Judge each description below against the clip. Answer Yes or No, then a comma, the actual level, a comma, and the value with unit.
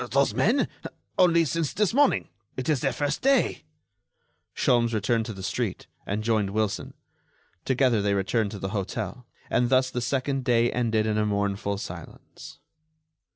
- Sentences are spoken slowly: No, average, 155 wpm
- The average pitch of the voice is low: Yes, low, 120 Hz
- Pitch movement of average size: Yes, average, 4.6 semitones